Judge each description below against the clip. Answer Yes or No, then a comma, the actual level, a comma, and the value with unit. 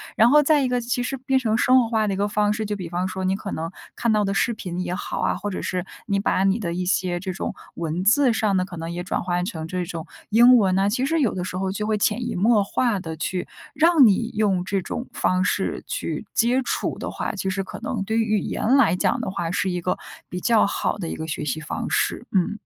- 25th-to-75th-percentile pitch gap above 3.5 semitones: Yes, average, 4.0 semitones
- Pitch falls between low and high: No, high, 195 Hz